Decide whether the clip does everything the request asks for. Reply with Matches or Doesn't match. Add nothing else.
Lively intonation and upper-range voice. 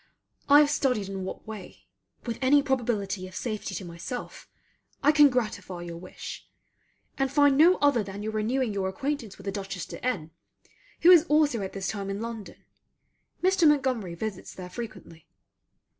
Matches